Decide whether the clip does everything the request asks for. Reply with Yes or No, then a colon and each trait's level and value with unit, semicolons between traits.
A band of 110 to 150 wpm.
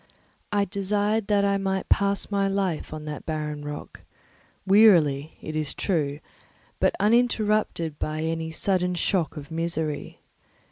Yes: slow, 135 wpm